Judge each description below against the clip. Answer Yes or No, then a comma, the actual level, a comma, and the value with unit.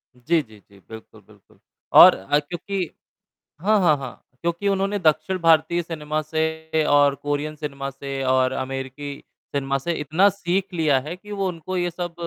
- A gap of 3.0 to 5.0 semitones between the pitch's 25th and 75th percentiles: Yes, average, 4.1 semitones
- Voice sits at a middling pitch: Yes, medium, 155 Hz